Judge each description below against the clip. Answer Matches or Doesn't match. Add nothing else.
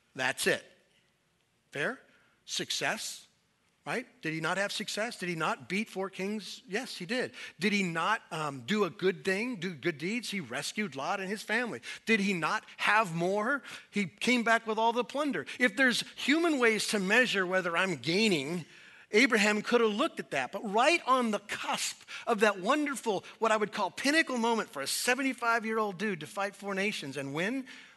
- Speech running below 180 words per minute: Doesn't match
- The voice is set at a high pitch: Matches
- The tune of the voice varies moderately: Matches